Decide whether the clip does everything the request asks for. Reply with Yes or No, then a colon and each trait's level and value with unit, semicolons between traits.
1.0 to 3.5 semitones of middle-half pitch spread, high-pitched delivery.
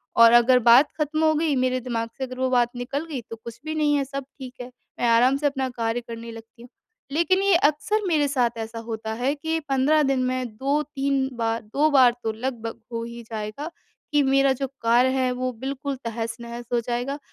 Yes: average, 3.2 semitones; very high, 255 Hz